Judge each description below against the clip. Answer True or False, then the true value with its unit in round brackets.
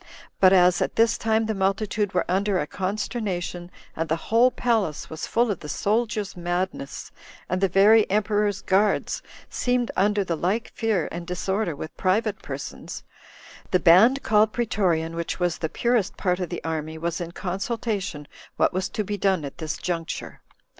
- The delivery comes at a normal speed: True (170 wpm)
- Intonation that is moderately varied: True (3.6 semitones)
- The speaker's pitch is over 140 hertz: True (190 Hz)